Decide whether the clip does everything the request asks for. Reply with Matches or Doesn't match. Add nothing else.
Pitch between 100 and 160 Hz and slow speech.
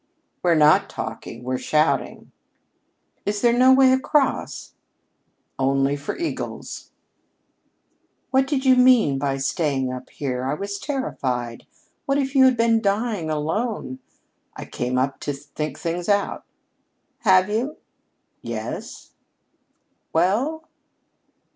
Doesn't match